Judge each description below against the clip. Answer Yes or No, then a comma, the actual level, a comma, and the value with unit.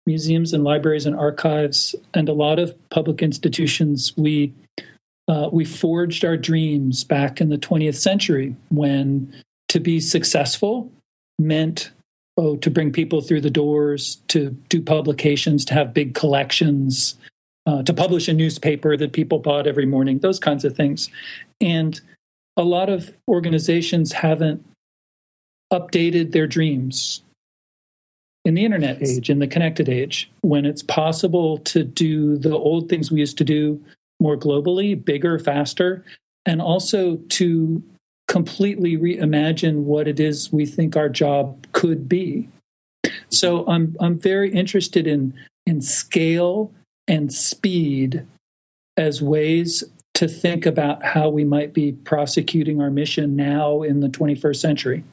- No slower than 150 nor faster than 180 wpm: No, average, 140 wpm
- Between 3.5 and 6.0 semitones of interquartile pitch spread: No, average, 2.7 semitones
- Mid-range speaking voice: Yes, medium, 155 Hz